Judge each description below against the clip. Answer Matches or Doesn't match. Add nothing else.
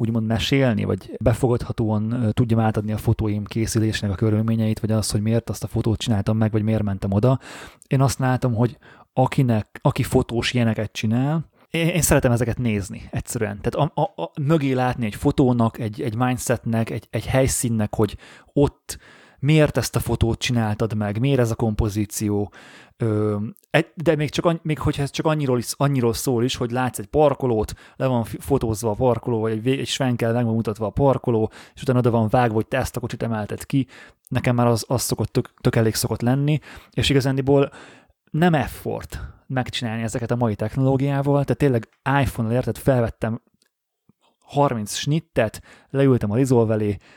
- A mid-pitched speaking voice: Doesn't match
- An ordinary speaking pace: Doesn't match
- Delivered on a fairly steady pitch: Doesn't match